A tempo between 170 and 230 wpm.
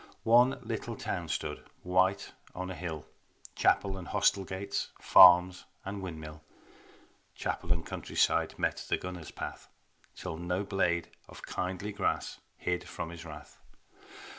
No: slow, 135 wpm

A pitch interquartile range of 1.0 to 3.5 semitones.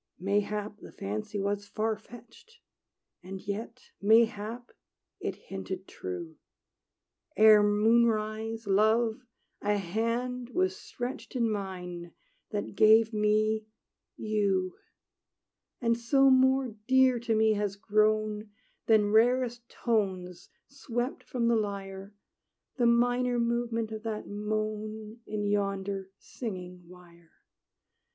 Yes: narrow, 2.6 semitones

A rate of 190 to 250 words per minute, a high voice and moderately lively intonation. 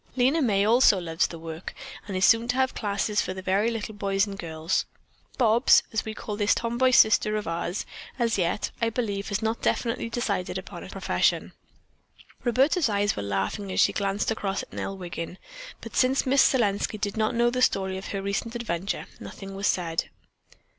Yes: average, 195 wpm; high, 205 Hz; average, 3.4 semitones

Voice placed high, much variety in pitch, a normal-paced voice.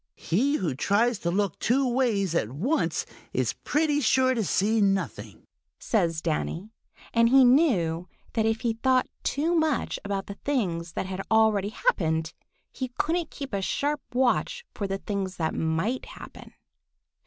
Yes: high, 220 Hz; wide, 5.7 semitones; average, 155 wpm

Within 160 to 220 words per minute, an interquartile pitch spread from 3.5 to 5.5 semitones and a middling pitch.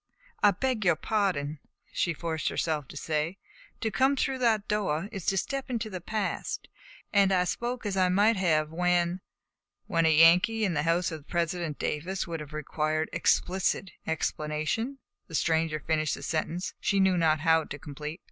Yes: average, 175 wpm; average, 4.2 semitones; medium, 175 Hz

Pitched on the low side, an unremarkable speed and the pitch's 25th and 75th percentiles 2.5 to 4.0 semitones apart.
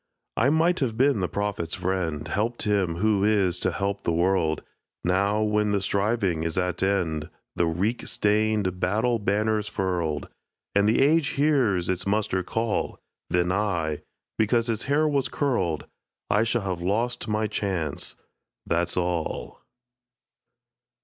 Yes: low, 100 Hz; average, 145 wpm; average, 3.6 semitones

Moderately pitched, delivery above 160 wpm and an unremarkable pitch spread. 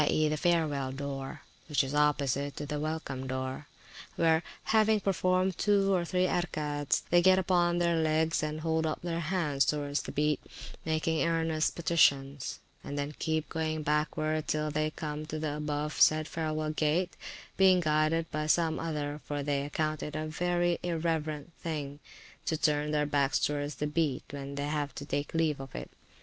No: medium, 155 Hz; average, 170 wpm; narrow, 2.1 semitones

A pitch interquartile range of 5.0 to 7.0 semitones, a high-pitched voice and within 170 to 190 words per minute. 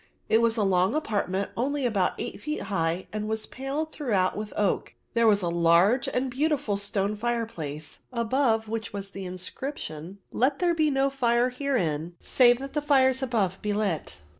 Yes: wide, 5.4 semitones; high, 220 Hz; average, 175 wpm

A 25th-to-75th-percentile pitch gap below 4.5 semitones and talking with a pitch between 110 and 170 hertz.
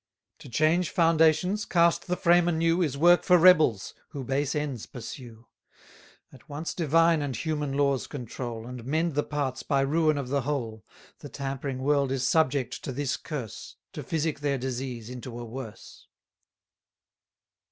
Yes: average, 3.8 semitones; medium, 140 Hz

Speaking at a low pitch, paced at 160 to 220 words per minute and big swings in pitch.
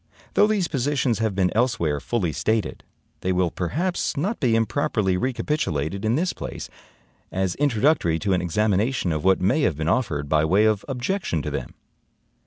Yes: low, 105 Hz; average, 170 wpm; wide, 6.9 semitones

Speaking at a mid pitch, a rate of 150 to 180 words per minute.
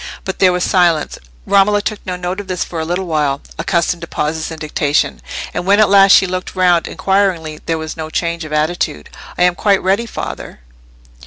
No: medium, 175 Hz; average, 200 wpm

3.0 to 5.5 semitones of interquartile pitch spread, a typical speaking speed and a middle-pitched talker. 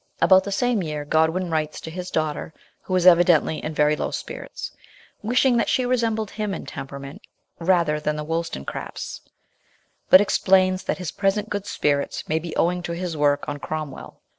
Yes: average, 4.1 semitones; average, 175 wpm; medium, 170 Hz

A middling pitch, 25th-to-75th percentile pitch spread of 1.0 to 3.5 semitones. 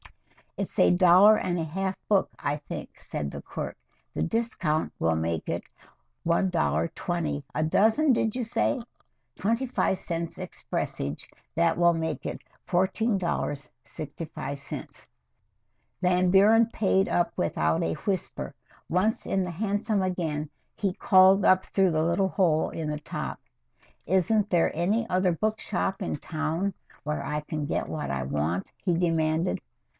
No: medium, 175 Hz; average, 4.1 semitones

